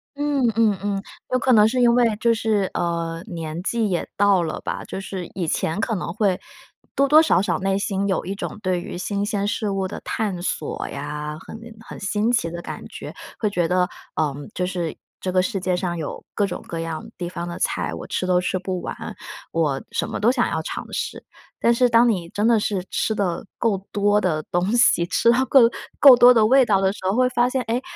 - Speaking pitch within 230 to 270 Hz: No, high, 195 Hz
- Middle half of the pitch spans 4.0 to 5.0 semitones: Yes, average, 4.3 semitones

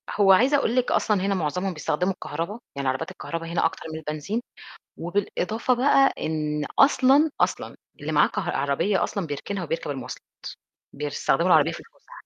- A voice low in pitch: No, medium, 180 Hz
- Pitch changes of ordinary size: No, wide, 6.2 semitones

